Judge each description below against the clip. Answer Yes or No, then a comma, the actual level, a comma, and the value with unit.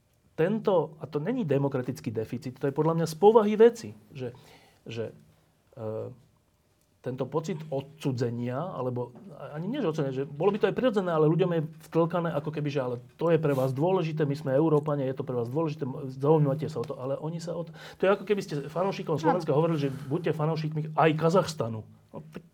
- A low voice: No, medium, 150 Hz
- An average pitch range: Yes, average, 3.7 semitones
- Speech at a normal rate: No, fast, 195 wpm